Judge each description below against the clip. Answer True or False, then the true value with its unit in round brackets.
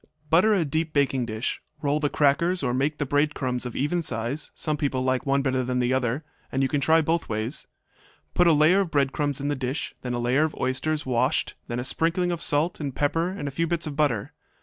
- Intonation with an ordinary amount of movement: True (3.5 semitones)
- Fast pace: True (235 wpm)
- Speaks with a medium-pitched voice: True (145 Hz)